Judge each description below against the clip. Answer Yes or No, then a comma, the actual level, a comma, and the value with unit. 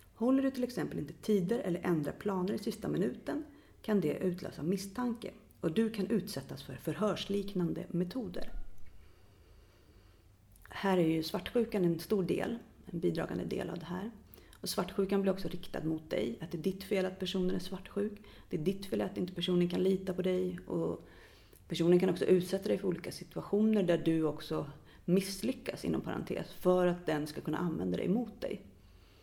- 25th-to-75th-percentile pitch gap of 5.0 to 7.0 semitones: No, average, 3.6 semitones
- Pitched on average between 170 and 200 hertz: Yes, medium, 185 Hz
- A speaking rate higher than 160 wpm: Yes, average, 180 wpm